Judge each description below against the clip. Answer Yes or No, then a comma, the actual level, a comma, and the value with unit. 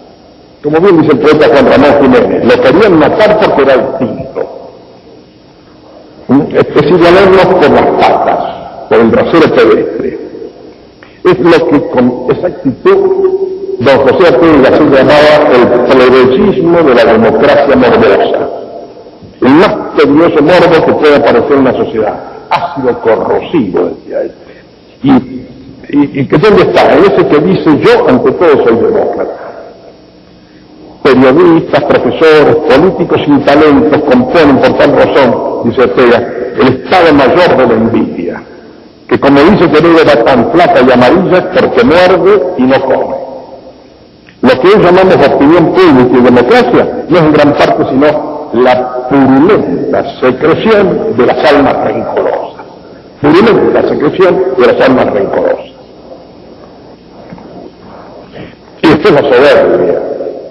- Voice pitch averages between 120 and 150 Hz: No, medium, 185 Hz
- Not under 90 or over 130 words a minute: No, average, 140 wpm